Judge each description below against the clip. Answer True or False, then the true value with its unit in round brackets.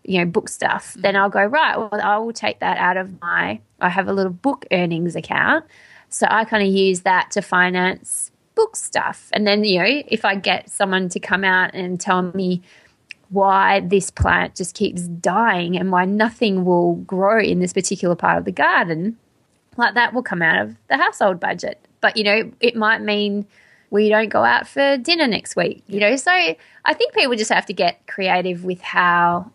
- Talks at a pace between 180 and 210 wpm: True (205 wpm)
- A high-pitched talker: True (195 Hz)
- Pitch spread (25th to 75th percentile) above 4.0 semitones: False (3.2 semitones)